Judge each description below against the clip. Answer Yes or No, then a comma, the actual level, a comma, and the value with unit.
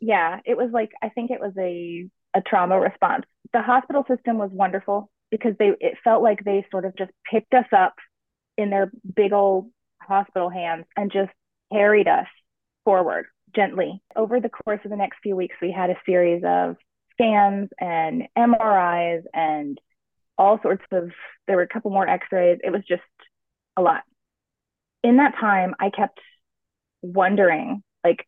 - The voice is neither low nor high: No, high, 200 Hz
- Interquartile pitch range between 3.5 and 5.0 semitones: Yes, average, 4.0 semitones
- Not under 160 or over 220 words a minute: Yes, average, 170 wpm